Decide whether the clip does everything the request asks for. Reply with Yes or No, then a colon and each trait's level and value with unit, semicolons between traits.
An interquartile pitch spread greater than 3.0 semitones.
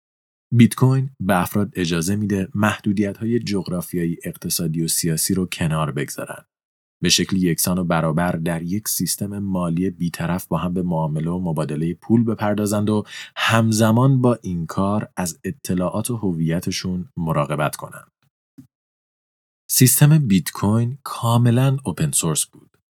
Yes: average, 4.3 semitones